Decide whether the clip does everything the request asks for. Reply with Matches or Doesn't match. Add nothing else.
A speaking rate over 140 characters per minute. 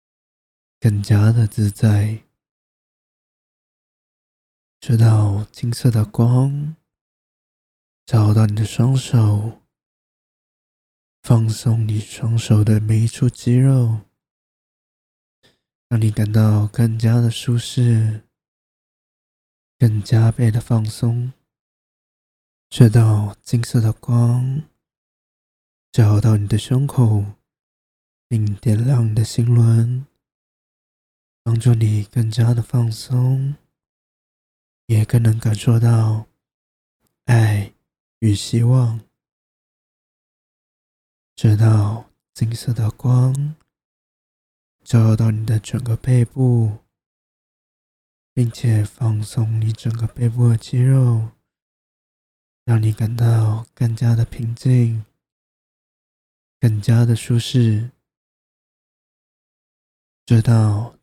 Doesn't match